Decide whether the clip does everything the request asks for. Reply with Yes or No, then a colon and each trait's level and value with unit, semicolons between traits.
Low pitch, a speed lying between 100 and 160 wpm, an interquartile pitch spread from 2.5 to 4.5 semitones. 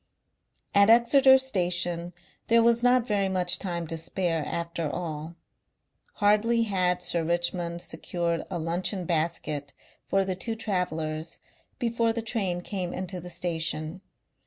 No: medium, 180 Hz; slow, 135 wpm; average, 3.6 semitones